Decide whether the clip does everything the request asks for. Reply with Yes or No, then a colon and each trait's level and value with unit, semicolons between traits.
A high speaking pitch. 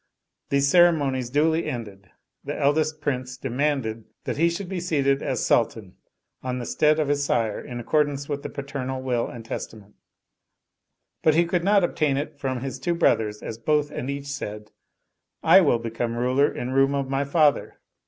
No: medium, 140 Hz